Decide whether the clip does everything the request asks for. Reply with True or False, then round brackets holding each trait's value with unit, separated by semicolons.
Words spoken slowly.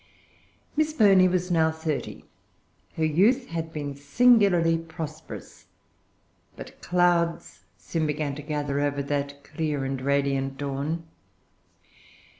True (110 wpm)